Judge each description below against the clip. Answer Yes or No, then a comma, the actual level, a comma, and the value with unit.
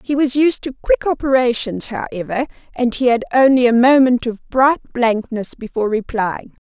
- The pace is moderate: Yes, average, 160 wpm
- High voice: Yes, high, 245 Hz